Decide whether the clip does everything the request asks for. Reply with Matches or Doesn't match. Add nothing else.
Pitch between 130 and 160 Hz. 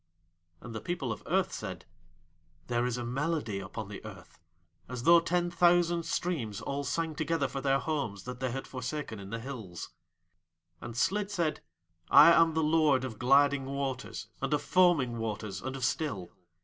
Matches